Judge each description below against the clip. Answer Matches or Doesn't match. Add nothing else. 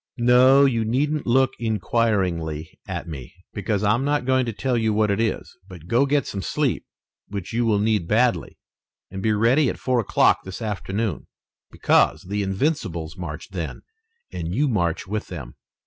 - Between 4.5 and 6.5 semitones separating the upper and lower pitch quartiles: Matches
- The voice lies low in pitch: Matches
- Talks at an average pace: Matches